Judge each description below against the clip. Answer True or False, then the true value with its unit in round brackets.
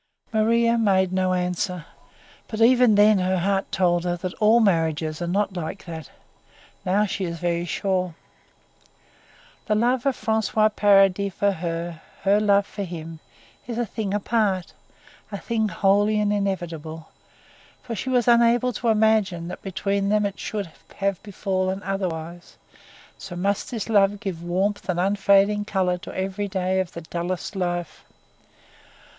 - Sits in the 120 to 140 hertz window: False (195 Hz)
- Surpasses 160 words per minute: False (150 wpm)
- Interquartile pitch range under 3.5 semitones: True (2.9 semitones)